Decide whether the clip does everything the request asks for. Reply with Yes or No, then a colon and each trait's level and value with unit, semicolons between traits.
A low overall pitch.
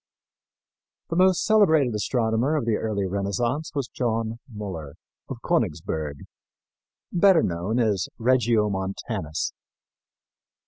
Yes: low, 110 Hz